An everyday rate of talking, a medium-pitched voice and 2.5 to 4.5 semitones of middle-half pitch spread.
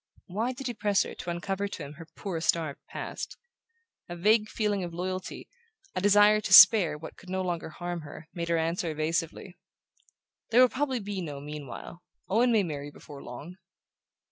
Yes: average, 180 wpm; medium, 180 Hz; average, 4.2 semitones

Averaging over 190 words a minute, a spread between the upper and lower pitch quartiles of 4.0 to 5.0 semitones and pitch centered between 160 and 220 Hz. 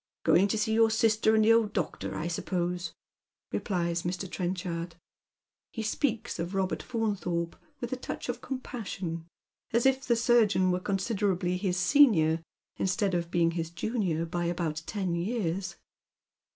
No: average, 150 wpm; average, 4.3 semitones; high, 190 Hz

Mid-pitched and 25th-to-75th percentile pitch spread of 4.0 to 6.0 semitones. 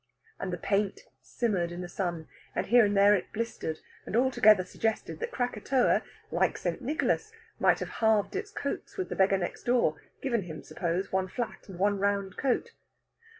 No: high, 205 Hz; average, 4.6 semitones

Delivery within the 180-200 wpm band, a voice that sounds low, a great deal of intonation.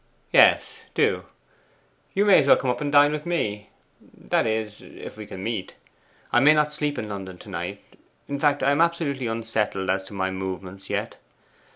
Yes: average, 185 wpm; low, 115 Hz; wide, 6.9 semitones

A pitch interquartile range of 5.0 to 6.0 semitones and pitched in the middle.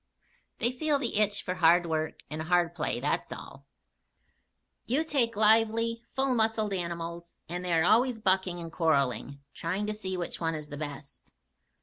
Yes: average, 5.3 semitones; medium, 180 Hz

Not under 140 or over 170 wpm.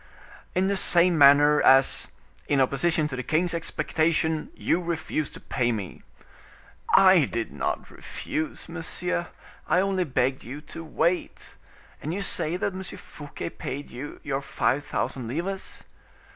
Yes: average, 145 wpm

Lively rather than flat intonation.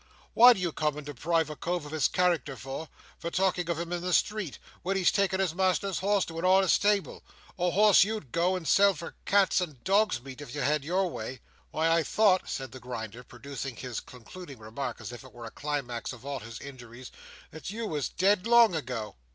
Yes: wide, 6.2 semitones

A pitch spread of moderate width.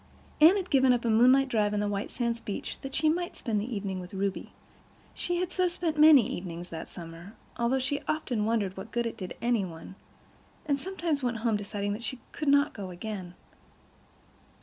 No: wide, 5.8 semitones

